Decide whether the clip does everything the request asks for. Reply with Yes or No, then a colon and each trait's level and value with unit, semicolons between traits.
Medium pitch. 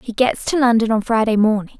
No: high, 225 Hz